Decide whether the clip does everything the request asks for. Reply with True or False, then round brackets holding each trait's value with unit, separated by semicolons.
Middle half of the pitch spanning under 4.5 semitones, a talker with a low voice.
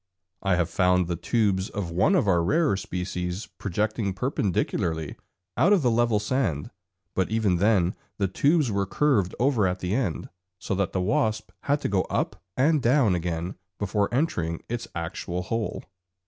False (4.8 semitones; 100 Hz)